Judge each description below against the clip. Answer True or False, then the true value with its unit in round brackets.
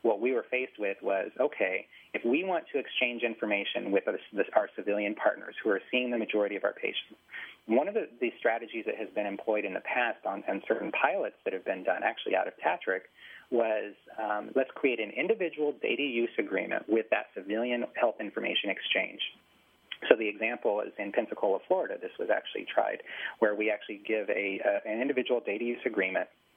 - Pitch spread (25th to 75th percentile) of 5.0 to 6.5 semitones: True (5.3 semitones)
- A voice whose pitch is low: True (120 Hz)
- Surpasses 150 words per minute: True (200 wpm)